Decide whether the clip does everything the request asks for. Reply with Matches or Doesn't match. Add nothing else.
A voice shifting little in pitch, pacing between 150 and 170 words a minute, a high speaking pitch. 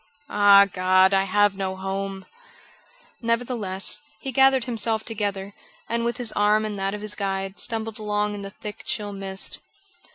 Matches